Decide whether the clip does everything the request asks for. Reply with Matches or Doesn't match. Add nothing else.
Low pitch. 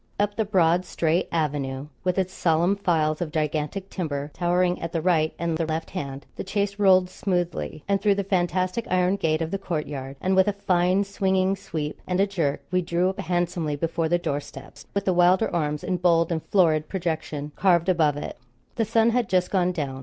Doesn't match